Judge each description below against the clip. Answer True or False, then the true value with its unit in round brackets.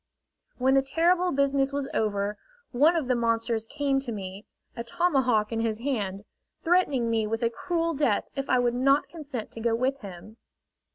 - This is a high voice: True (250 Hz)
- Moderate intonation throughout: True (3.9 semitones)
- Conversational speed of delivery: True (180 wpm)